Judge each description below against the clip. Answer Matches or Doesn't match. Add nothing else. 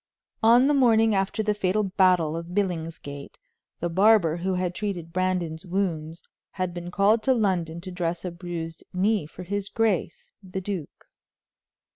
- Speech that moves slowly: Doesn't match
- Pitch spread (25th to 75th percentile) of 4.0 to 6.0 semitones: Doesn't match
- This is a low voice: Doesn't match